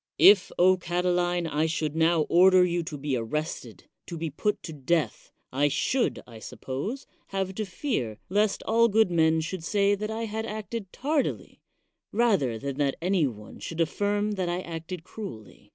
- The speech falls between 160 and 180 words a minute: Yes, average, 170 wpm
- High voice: No, medium, 175 Hz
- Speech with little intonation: No, average, 5.1 semitones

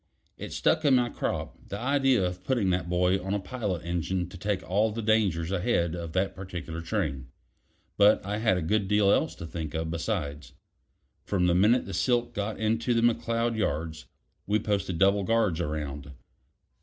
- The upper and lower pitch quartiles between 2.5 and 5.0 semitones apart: Yes, average, 4.3 semitones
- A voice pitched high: No, very low, 95 Hz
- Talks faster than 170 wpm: Yes, average, 180 wpm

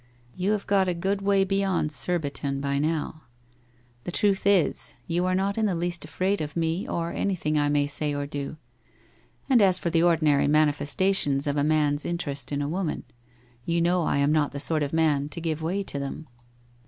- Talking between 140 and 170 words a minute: No, fast, 205 wpm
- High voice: No, medium, 165 Hz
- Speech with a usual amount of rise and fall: Yes, average, 4.1 semitones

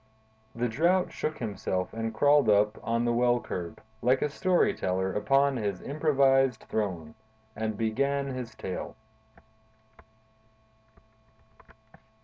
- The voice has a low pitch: Yes, low, 120 Hz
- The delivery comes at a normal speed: No, slow, 115 wpm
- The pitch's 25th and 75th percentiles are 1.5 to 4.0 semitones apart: No, average, 4.7 semitones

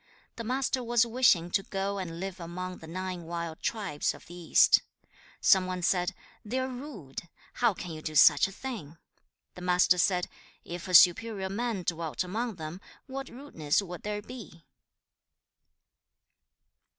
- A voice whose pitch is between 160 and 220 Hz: Yes, medium, 185 Hz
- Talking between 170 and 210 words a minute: No, average, 160 wpm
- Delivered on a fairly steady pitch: No, average, 4.8 semitones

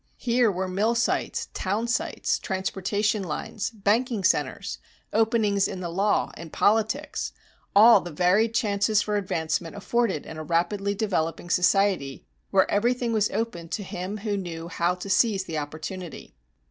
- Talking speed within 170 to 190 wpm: No, average, 145 wpm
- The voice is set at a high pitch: Yes, high, 200 Hz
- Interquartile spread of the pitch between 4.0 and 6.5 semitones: No, average, 3.5 semitones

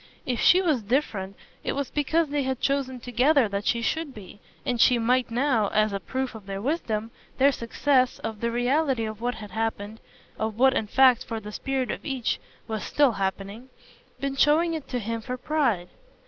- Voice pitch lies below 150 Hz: No, high, 245 Hz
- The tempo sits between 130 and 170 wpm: No, average, 195 wpm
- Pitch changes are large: No, average, 3.9 semitones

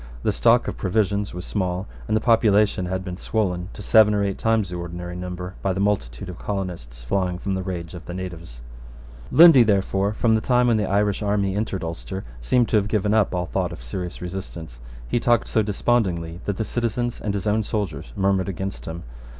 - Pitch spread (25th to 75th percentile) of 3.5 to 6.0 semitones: No, average, 3.1 semitones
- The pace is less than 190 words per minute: No, fast, 205 wpm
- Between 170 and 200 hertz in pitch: No, very low, 95 Hz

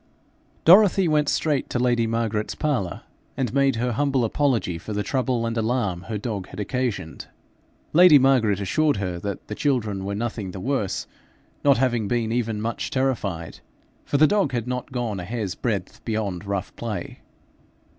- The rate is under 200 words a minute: Yes, average, 165 wpm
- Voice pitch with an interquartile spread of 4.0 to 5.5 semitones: Yes, average, 4.5 semitones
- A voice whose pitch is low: Yes, low, 115 Hz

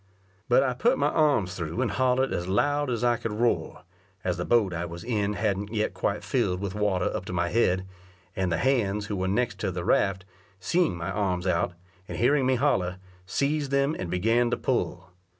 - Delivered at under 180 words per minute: No, fast, 205 wpm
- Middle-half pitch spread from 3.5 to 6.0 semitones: Yes, average, 5.3 semitones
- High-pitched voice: No, low, 105 Hz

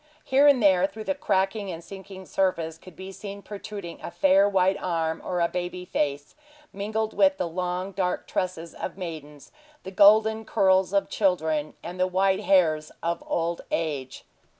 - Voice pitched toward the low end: No, medium, 185 Hz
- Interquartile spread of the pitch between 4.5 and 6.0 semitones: No, average, 2.8 semitones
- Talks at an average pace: Yes, average, 170 wpm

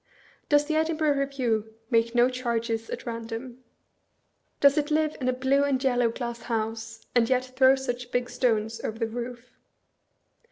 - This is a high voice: Yes, high, 245 Hz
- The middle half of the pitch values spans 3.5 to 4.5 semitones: No, narrow, 2.6 semitones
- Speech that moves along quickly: No, average, 160 wpm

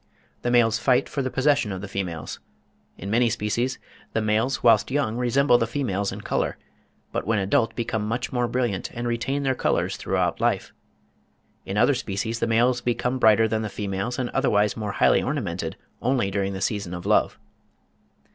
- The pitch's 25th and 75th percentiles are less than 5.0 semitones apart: Yes, average, 3.2 semitones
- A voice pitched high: No, low, 115 Hz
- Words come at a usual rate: Yes, average, 180 wpm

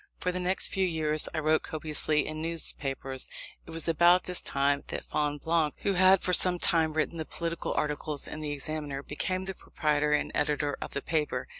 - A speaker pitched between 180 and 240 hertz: No, medium, 155 Hz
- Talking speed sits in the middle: Yes, average, 190 wpm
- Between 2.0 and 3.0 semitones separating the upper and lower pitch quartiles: Yes, narrow, 2.4 semitones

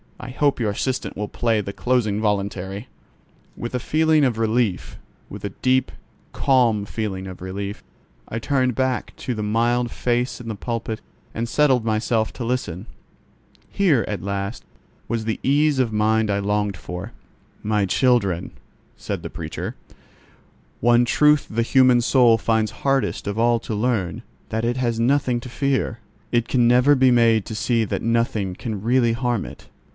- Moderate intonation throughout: Yes, average, 3.1 semitones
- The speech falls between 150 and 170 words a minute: Yes, average, 160 wpm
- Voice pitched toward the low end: Yes, low, 115 Hz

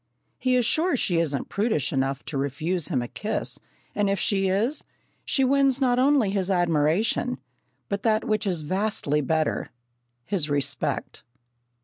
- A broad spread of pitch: Yes, wide, 7.1 semitones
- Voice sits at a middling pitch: No, high, 195 Hz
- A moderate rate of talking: Yes, average, 150 wpm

